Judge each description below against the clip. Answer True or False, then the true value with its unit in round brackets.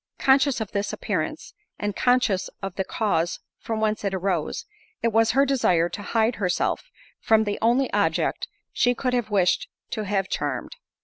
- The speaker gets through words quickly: False (170 wpm)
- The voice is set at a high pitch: True (215 Hz)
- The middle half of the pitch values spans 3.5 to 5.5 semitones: True (3.8 semitones)